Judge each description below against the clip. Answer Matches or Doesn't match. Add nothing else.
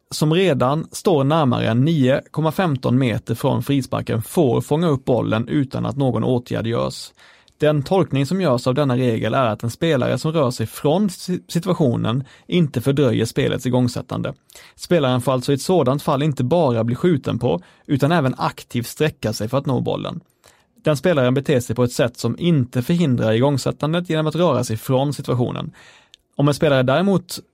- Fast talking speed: Doesn't match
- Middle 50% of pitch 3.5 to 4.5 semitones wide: Matches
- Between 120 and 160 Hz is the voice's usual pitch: Matches